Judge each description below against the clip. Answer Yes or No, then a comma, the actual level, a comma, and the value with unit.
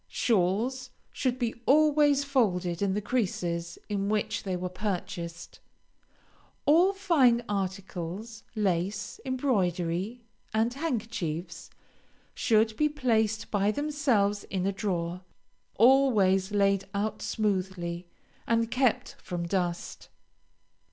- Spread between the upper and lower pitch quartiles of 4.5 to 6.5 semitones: Yes, average, 5.2 semitones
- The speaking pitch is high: Yes, high, 210 Hz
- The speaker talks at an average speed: No, slow, 105 wpm